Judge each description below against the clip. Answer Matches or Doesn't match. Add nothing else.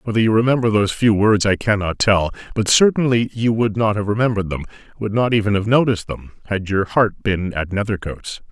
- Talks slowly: Doesn't match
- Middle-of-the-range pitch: Doesn't match